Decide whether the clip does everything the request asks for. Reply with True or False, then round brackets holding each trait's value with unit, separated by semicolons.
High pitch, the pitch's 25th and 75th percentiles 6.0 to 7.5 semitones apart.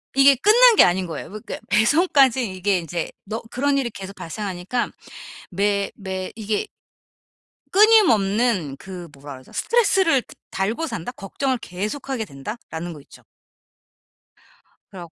True (210 Hz; 6.7 semitones)